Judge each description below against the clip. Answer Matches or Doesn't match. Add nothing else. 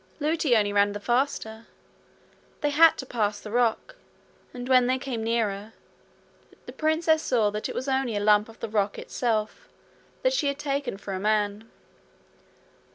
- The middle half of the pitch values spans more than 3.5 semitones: Matches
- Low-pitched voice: Doesn't match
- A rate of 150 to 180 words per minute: Matches